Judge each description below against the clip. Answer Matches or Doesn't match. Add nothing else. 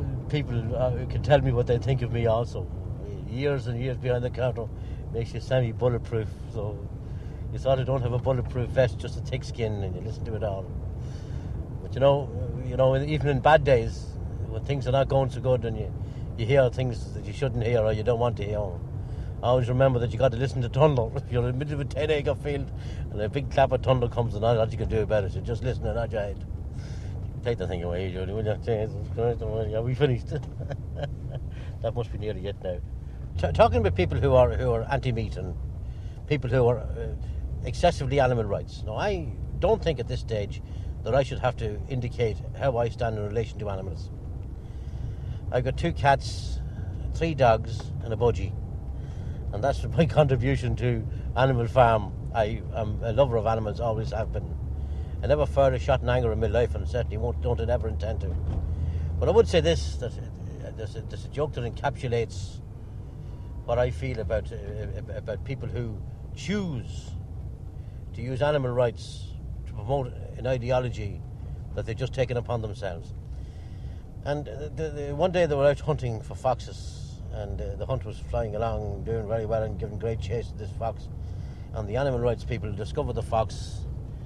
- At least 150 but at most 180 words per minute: Doesn't match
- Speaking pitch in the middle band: Doesn't match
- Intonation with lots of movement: Doesn't match